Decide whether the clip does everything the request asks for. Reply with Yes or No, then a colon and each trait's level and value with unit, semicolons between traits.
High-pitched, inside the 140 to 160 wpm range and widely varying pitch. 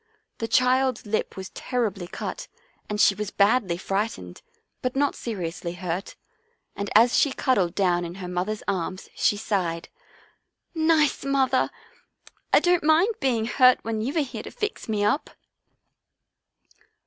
Yes: high, 220 Hz; average, 150 wpm; wide, 5.7 semitones